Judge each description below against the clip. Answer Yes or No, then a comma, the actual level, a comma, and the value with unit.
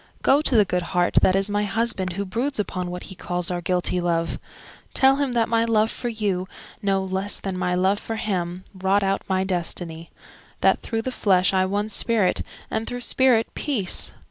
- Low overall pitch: No, high, 195 Hz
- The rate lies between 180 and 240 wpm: Yes, average, 195 wpm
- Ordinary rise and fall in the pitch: Yes, average, 3.6 semitones